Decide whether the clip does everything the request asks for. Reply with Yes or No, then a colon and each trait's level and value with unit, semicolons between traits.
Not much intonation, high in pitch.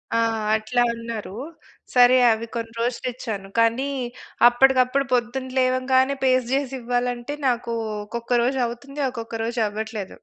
Yes: narrow, 1.9 semitones; high, 245 Hz